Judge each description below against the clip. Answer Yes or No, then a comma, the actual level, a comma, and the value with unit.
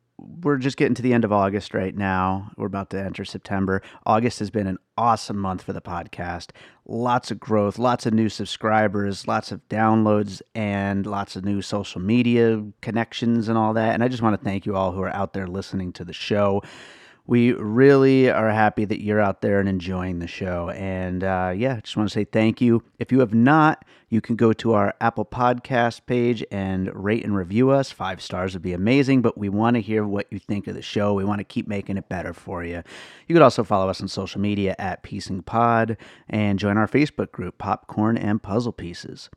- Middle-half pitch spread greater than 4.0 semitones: No, average, 3.1 semitones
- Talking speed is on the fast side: Yes, fast, 215 wpm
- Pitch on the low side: Yes, low, 105 Hz